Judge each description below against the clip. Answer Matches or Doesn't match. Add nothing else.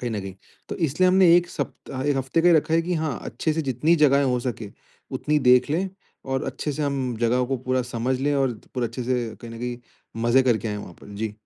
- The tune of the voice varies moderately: Matches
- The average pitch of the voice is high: Doesn't match